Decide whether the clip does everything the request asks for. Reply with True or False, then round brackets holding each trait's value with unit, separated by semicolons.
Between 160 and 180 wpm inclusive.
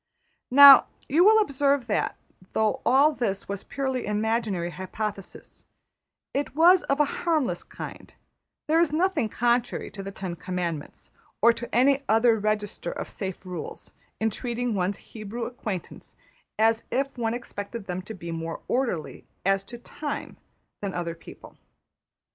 False (145 wpm)